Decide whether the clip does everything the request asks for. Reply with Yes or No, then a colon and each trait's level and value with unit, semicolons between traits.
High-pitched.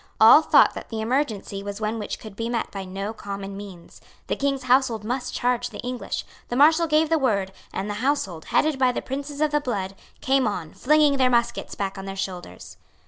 Yes: high, 235 Hz